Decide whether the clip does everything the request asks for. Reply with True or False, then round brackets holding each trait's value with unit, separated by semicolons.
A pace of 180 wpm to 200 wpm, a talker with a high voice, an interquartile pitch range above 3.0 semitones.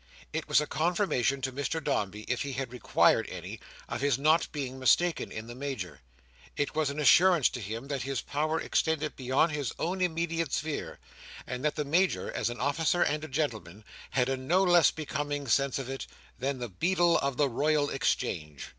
False (190 wpm; 140 Hz; 3.7 semitones)